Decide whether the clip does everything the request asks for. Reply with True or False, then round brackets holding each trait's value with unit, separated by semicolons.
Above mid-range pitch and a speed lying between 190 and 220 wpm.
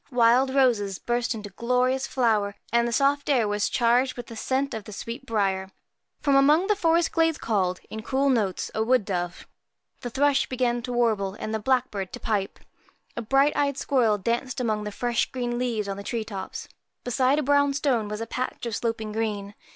True (235 Hz; 195 wpm)